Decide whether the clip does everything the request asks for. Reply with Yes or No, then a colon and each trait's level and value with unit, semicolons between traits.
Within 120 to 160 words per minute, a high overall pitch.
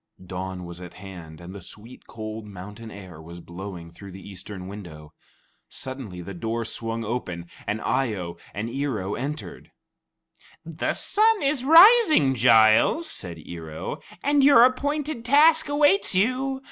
No: average, 150 wpm; low, 110 Hz